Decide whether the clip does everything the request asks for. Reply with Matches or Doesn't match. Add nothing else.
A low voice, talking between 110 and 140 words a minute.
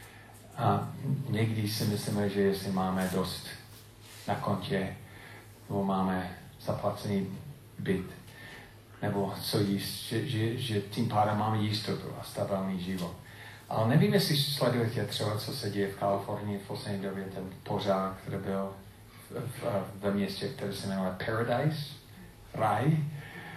Matches